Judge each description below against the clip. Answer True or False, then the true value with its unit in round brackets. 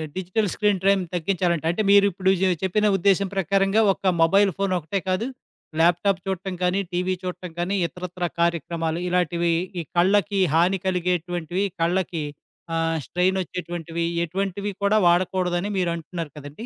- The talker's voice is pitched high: False (180 Hz)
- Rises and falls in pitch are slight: True (2.2 semitones)